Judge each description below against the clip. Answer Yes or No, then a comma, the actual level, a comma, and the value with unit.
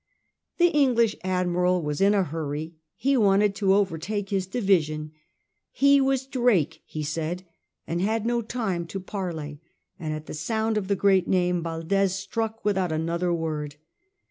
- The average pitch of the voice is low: No, medium, 185 Hz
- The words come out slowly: No, average, 155 wpm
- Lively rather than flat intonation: No, average, 4.4 semitones